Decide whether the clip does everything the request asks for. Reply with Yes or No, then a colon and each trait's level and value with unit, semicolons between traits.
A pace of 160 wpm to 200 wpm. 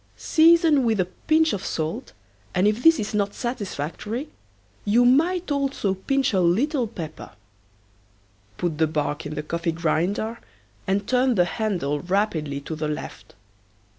No: average, 145 wpm